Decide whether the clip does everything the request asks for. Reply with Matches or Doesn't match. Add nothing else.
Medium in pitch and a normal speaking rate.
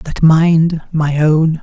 Matches